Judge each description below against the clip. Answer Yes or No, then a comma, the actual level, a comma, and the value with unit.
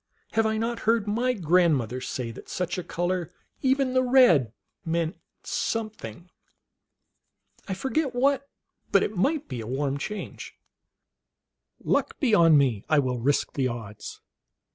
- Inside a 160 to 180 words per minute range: No, average, 140 wpm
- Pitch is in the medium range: Yes, medium, 180 Hz